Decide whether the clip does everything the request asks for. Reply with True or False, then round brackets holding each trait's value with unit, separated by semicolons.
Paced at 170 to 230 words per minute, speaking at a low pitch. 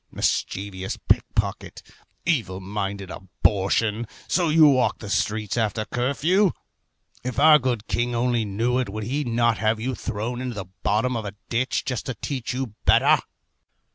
False (160 wpm; 115 Hz)